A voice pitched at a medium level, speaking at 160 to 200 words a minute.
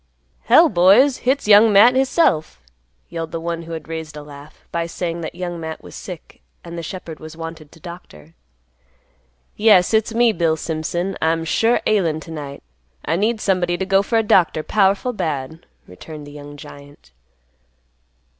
Yes: medium, 170 Hz; average, 170 wpm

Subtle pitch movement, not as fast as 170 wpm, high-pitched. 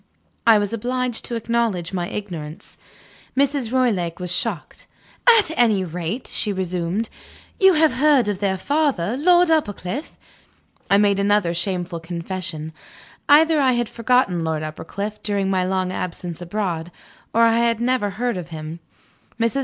No: wide, 5.6 semitones; average, 145 wpm; high, 205 Hz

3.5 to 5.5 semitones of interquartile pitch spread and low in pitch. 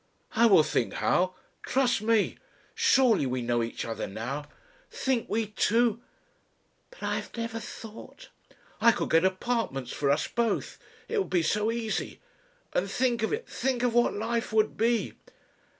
No: average, 4.5 semitones; high, 225 Hz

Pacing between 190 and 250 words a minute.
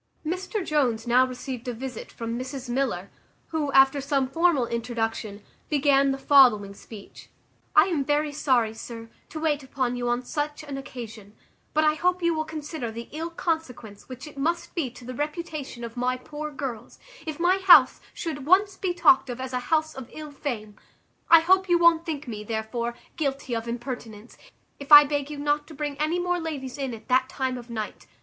Yes: average, 195 wpm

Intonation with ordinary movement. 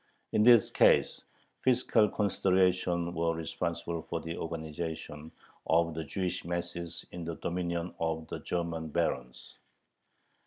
No: narrow, 1.5 semitones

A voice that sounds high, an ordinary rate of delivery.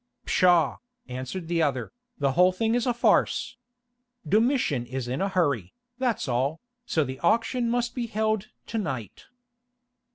No: medium, 175 Hz; average, 150 wpm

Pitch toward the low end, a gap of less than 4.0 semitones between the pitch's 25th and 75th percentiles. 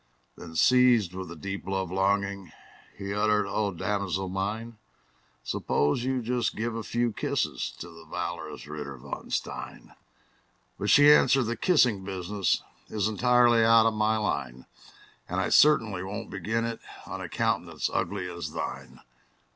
Yes: low, 105 Hz; average, 3.6 semitones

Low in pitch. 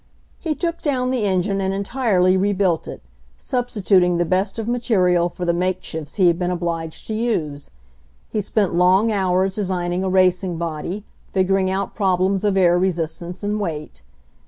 No: medium, 185 Hz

